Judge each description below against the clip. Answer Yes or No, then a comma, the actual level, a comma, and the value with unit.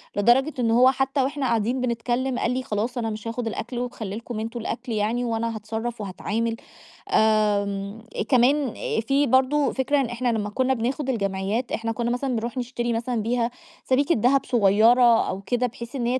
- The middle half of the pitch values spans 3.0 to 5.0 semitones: No, narrow, 2.5 semitones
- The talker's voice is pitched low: No, high, 235 Hz